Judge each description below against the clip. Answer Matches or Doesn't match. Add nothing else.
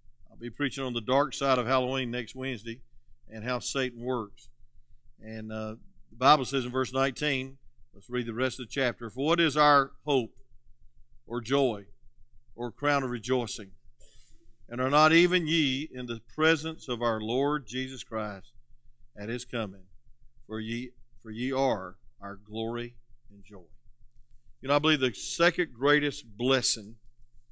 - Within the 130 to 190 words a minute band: Matches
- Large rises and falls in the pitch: Doesn't match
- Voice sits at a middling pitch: Doesn't match